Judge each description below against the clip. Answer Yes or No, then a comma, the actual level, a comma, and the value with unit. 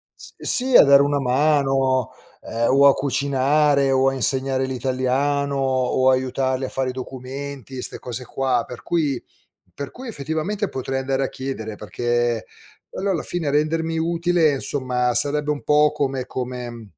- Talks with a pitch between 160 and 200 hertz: No, low, 135 Hz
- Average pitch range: No, narrow, 2.2 semitones